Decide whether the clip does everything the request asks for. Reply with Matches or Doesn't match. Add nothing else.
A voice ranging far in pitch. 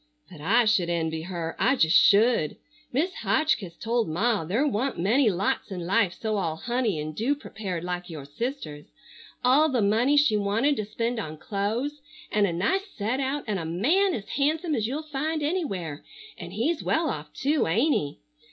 Matches